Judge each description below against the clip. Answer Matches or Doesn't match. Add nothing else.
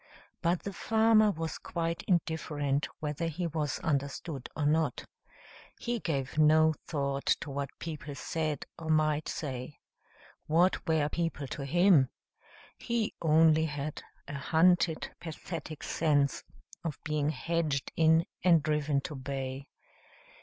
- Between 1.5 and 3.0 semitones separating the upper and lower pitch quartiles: Matches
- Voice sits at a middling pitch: Matches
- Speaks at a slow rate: Matches